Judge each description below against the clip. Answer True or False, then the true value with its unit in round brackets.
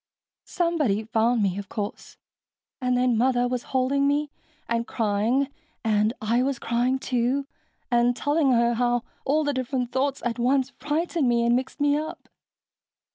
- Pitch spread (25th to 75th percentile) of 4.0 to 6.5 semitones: False (2.9 semitones)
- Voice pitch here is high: True (250 Hz)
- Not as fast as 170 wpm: True (155 wpm)